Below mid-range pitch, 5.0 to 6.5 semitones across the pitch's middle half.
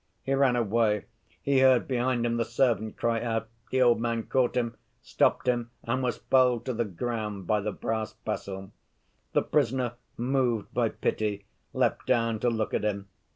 No: low, 115 Hz; narrow, 2.5 semitones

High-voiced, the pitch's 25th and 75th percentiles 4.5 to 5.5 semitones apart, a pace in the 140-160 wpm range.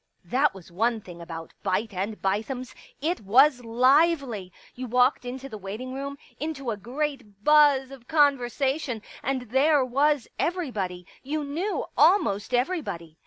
Yes: very high, 255 Hz; average, 5.2 semitones; average, 150 wpm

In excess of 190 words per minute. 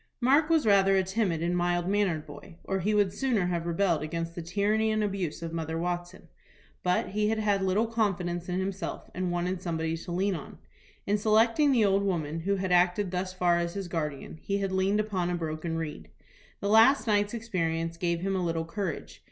Yes: average, 200 wpm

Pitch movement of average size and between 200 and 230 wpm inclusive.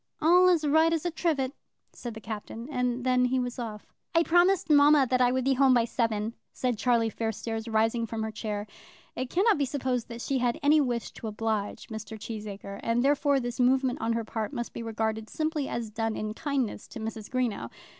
Yes: average, 3.7 semitones; fast, 205 wpm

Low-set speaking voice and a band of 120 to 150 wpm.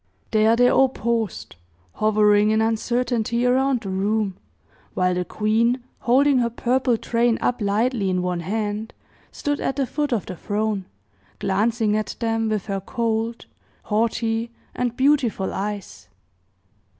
No: high, 225 Hz; average, 140 wpm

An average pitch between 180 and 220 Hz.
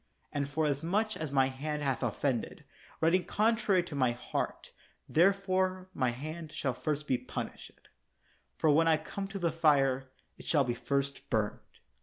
No: medium, 150 Hz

